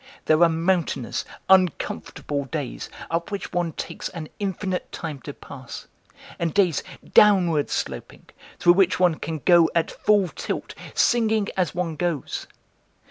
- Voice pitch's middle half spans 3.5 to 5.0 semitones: No, average, 3.1 semitones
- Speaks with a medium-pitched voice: Yes, medium, 170 Hz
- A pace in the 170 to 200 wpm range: No, slow, 135 wpm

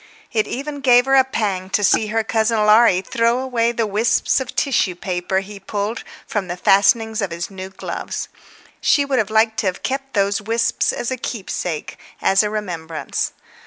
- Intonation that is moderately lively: Yes, average, 3.5 semitones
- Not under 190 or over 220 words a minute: No, average, 180 wpm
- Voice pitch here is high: Yes, high, 215 Hz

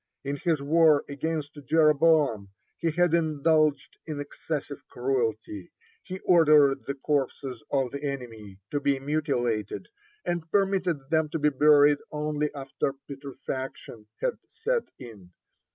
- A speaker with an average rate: No, slow, 125 wpm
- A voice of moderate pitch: Yes, medium, 145 Hz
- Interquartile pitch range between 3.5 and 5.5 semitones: No, average, 2.9 semitones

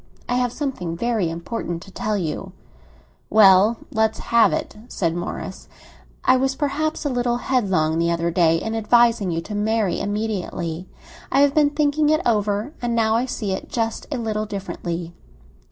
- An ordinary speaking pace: Yes, average, 170 wpm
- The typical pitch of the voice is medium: No, high, 220 Hz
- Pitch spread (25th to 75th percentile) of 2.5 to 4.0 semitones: No, average, 5.3 semitones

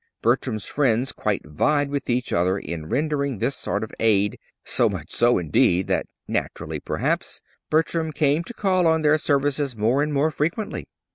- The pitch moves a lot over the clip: Yes, wide, 5.9 semitones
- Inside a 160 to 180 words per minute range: Yes, average, 165 wpm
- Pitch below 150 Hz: Yes, medium, 140 Hz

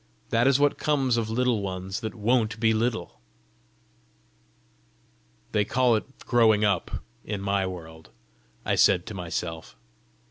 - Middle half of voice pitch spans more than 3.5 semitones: Yes, average, 3.9 semitones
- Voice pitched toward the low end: Yes, low, 110 Hz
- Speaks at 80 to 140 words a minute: Yes, slow, 135 wpm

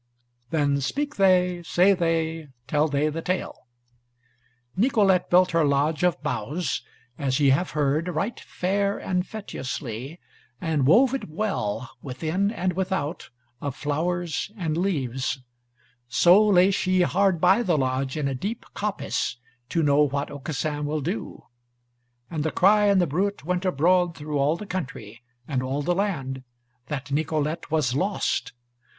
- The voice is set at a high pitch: No, medium, 160 Hz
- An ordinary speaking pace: Yes, average, 145 wpm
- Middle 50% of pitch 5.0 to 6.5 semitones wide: No, average, 4.6 semitones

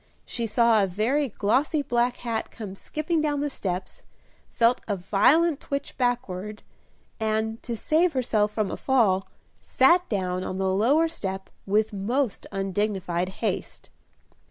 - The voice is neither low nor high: No, high, 220 Hz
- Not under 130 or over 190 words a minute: Yes, average, 140 wpm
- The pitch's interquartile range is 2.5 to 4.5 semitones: No, average, 5.3 semitones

